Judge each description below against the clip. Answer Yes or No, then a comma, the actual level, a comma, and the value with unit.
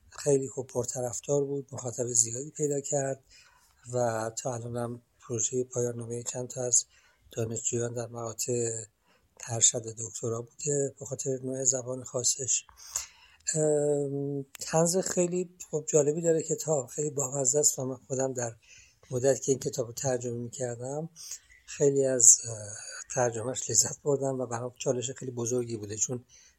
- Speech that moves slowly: No, average, 140 wpm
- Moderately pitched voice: No, low, 130 Hz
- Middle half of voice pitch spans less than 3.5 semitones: Yes, average, 2.8 semitones